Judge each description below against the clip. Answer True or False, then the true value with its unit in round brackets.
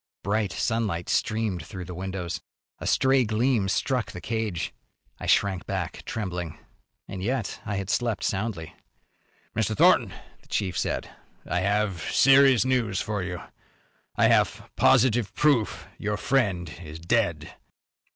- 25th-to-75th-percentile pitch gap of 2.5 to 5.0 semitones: True (4.1 semitones)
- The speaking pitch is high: False (105 Hz)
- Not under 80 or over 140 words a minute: True (135 wpm)